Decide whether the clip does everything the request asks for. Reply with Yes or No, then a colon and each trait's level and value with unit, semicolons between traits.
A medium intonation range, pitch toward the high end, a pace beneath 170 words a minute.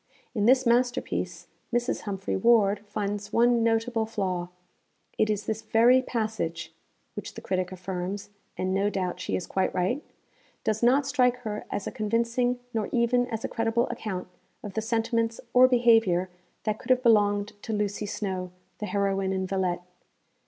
Yes: average, 3.3 semitones; high, 215 Hz; average, 160 wpm